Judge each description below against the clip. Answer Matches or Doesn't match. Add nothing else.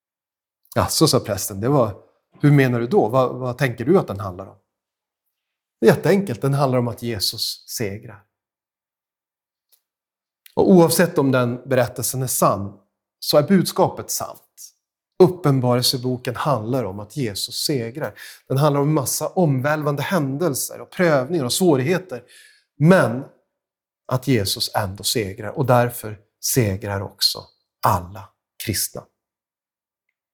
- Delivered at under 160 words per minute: Matches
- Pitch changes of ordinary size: Matches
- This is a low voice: Matches